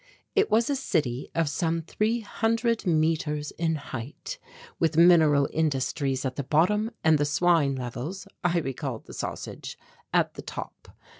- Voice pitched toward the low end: No, medium, 160 Hz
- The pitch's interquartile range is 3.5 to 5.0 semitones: Yes, average, 4.2 semitones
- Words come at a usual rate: Yes, average, 150 wpm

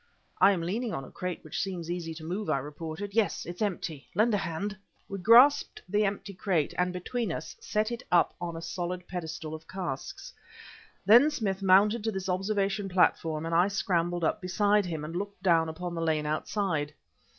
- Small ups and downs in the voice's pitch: No, average, 3.7 semitones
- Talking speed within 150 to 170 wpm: No, average, 195 wpm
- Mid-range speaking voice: Yes, medium, 180 Hz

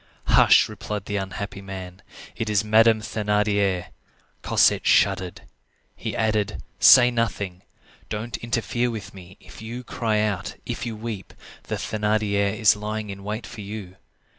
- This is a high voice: No, low, 105 Hz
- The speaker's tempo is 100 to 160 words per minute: Yes, average, 140 wpm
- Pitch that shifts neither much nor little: No, narrow, 1.9 semitones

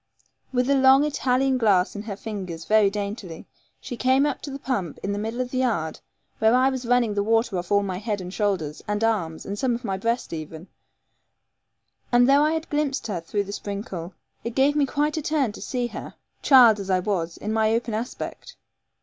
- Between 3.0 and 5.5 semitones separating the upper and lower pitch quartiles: Yes, average, 4.5 semitones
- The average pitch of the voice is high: Yes, high, 220 Hz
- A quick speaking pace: Yes, fast, 215 wpm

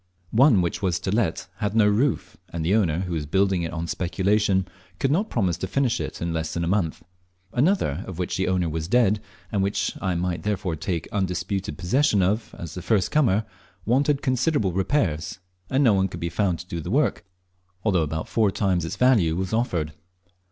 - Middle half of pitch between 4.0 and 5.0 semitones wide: Yes, average, 4.3 semitones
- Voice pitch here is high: No, very low, 95 Hz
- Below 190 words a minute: No, average, 200 wpm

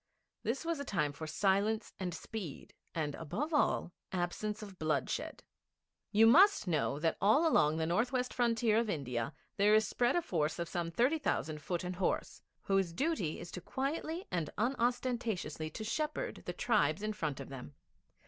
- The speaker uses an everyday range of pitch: No, wide, 7.1 semitones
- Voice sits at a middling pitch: No, high, 200 Hz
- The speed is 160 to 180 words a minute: Yes, average, 175 wpm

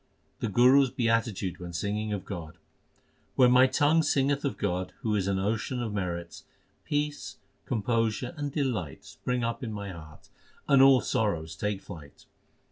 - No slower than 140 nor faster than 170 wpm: Yes, average, 160 wpm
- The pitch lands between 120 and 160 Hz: No, low, 110 Hz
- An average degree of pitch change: No, wide, 5.8 semitones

